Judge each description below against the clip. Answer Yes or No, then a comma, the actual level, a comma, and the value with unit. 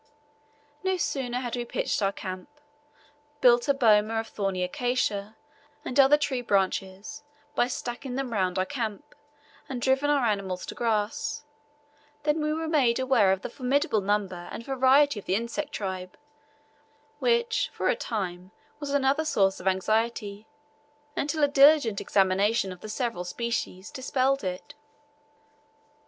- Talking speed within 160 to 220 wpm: No, average, 145 wpm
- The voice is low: No, high, 235 Hz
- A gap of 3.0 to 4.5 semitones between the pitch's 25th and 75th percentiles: No, wide, 5.6 semitones